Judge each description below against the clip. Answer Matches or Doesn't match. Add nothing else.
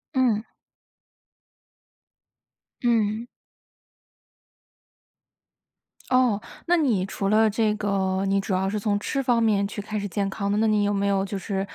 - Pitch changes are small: Matches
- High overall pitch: Matches